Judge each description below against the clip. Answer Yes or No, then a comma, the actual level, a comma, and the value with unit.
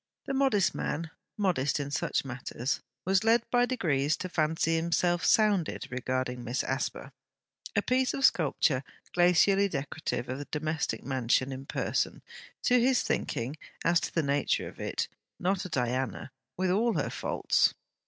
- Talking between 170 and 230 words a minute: No, average, 155 wpm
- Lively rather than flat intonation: Yes, wide, 6.7 semitones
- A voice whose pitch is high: No, medium, 160 Hz